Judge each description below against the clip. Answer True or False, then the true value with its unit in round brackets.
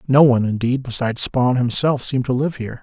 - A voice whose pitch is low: True (125 Hz)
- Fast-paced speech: True (215 wpm)